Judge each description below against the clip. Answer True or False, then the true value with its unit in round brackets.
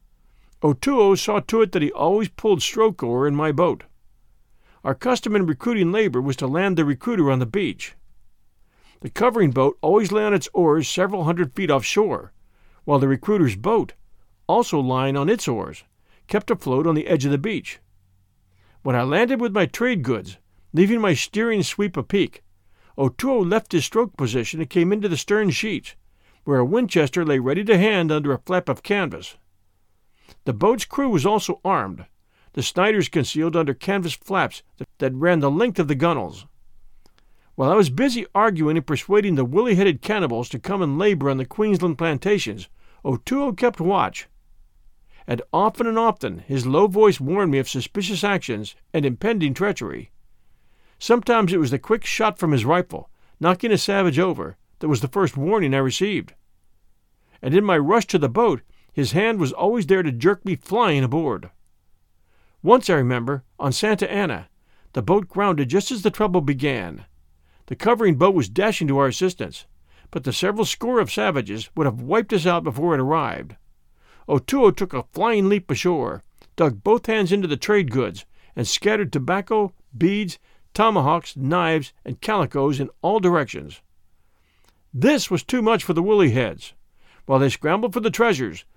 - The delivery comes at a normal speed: True (175 wpm)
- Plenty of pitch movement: True (7.5 semitones)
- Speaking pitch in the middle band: True (170 Hz)